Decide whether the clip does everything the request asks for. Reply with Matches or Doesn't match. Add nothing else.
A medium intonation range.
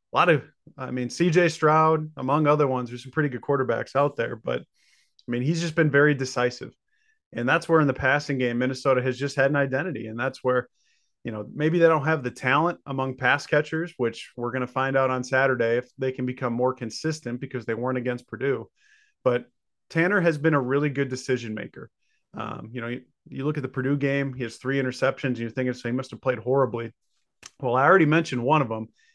Matches